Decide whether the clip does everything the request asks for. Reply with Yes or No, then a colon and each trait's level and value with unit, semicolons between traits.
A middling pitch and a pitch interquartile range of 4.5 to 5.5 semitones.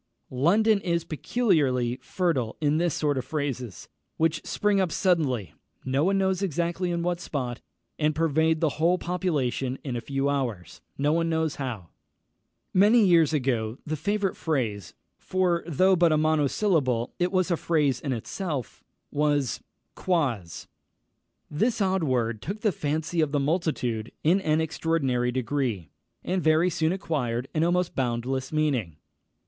Yes: medium, 155 Hz; average, 5.1 semitones